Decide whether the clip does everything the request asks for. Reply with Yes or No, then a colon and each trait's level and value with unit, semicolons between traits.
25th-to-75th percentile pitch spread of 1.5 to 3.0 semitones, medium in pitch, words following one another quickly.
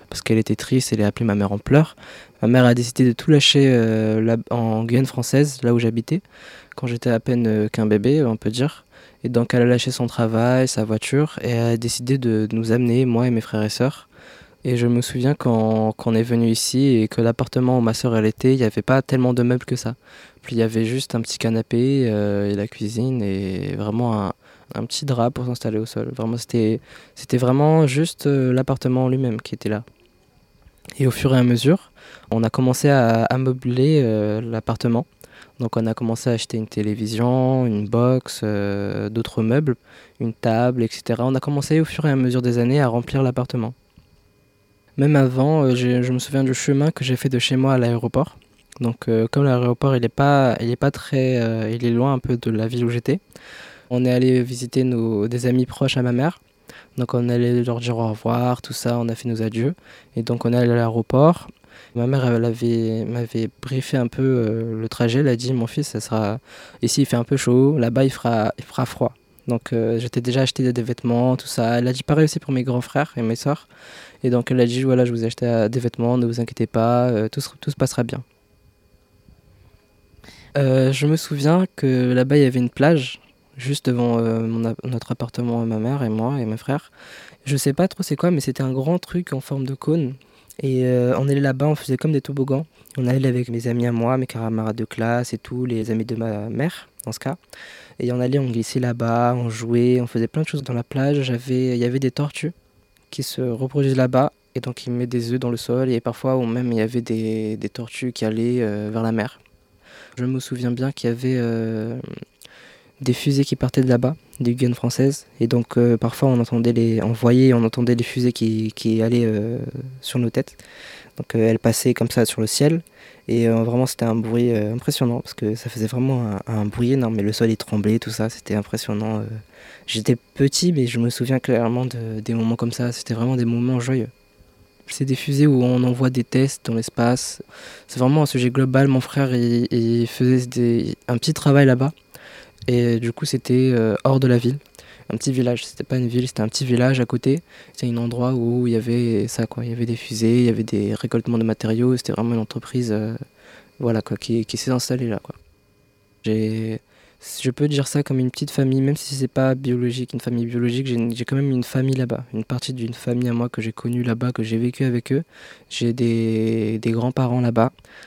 No: narrow, 2.4 semitones; low, 120 Hz; fast, 230 wpm